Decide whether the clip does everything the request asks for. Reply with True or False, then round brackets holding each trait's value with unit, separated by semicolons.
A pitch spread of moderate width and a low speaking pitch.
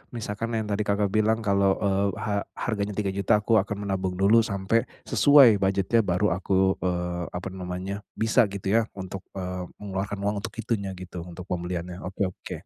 False (2.1 semitones; 100 Hz)